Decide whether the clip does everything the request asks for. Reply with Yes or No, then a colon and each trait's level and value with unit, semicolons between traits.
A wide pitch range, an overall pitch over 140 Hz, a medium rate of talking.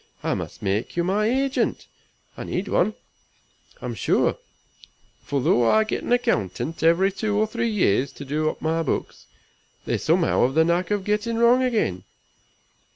Yes: wide, 5.9 semitones; medium, 185 Hz; average, 165 wpm